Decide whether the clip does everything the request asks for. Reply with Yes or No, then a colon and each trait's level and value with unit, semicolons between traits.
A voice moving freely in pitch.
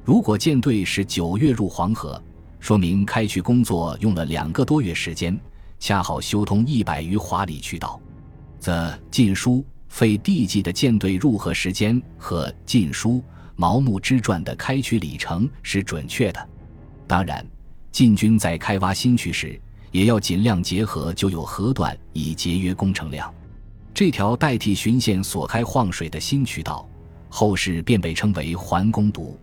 No: average, 4.8 semitones